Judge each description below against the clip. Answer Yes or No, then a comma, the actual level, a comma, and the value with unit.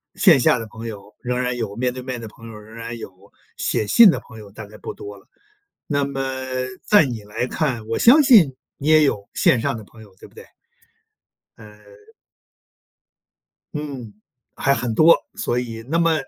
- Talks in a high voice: No, low, 120 Hz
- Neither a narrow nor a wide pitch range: Yes, average, 4.5 semitones